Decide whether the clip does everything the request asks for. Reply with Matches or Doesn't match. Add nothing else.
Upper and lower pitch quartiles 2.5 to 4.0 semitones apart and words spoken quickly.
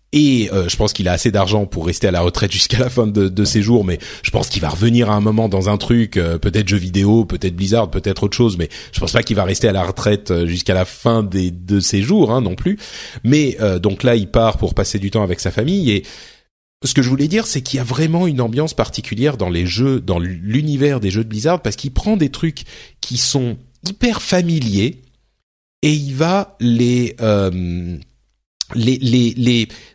Doesn't match